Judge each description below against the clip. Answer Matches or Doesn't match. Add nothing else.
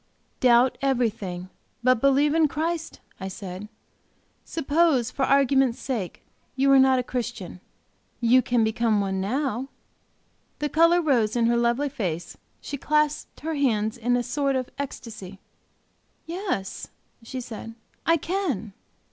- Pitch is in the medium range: Doesn't match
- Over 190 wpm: Doesn't match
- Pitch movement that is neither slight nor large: Matches